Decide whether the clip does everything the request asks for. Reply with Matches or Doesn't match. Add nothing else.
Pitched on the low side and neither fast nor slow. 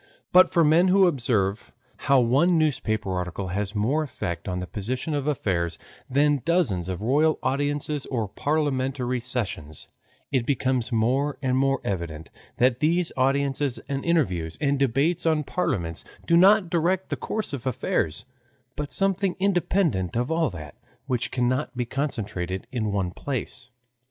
Matches